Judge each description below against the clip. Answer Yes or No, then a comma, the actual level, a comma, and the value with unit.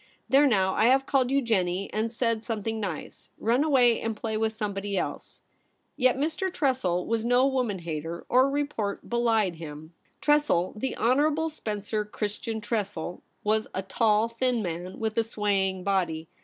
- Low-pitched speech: No, high, 220 Hz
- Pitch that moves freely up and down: No, average, 4.5 semitones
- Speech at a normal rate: Yes, average, 170 wpm